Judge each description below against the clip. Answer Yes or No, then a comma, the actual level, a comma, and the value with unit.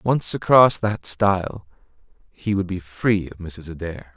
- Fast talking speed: No, average, 160 wpm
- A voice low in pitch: Yes, very low, 95 Hz